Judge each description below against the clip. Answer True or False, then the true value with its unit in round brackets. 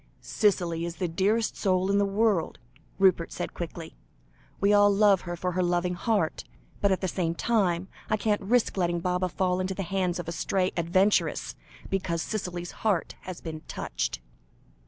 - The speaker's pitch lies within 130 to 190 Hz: True (185 Hz)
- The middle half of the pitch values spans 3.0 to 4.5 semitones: False (2.5 semitones)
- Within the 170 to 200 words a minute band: True (175 wpm)